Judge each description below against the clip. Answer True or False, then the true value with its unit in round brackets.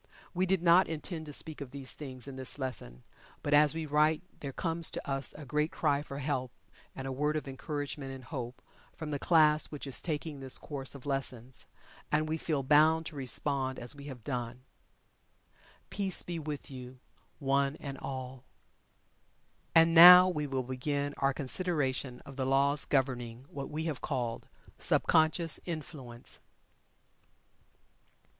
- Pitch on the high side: False (140 Hz)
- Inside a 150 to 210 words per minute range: True (165 wpm)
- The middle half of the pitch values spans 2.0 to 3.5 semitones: True (2.9 semitones)